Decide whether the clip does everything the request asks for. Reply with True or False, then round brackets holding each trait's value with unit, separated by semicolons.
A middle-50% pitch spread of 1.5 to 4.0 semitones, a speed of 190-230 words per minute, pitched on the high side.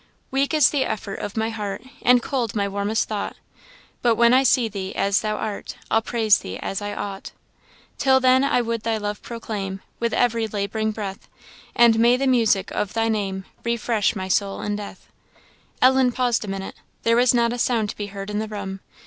True (2.9 semitones; 200 wpm; 220 Hz)